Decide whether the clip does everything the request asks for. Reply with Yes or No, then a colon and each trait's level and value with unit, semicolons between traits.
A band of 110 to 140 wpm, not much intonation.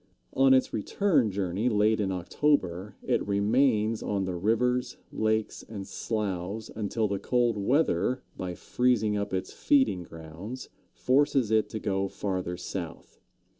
No: slow, 135 wpm; average, 4.4 semitones